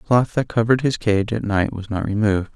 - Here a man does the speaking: Yes, male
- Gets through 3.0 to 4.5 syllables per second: No, 6.0 syllables/s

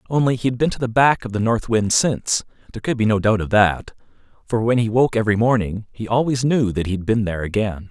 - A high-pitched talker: No, low, 110 Hz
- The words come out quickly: Yes, fast, 250 wpm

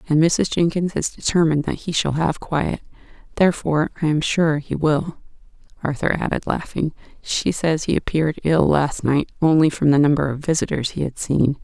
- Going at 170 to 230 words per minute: Yes, average, 180 wpm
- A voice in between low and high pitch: Yes, medium, 155 Hz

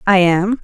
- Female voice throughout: Yes, female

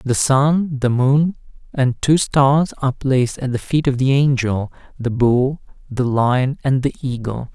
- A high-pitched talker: No, low, 130 Hz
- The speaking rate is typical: Yes, average, 175 wpm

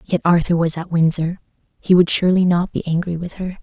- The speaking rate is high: Yes, fast, 215 wpm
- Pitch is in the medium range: Yes, medium, 175 Hz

